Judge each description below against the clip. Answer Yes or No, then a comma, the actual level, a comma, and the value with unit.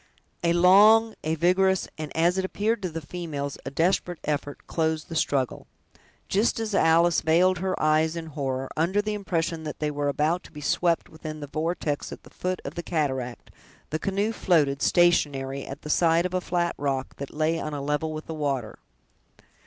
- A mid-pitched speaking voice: Yes, medium, 160 Hz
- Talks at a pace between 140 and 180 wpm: No, average, 190 wpm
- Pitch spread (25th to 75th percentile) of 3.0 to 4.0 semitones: Yes, average, 3.3 semitones